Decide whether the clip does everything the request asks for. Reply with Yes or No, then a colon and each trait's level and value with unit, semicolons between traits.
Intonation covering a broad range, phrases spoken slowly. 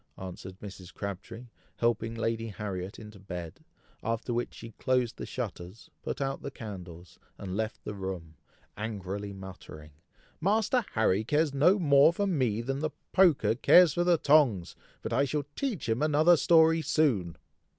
No: wide, 7.5 semitones; average, 155 wpm